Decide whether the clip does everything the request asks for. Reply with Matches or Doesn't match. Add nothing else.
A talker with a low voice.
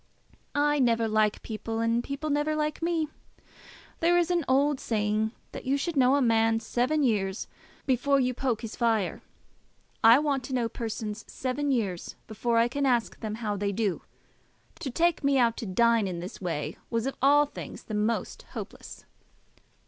Doesn't match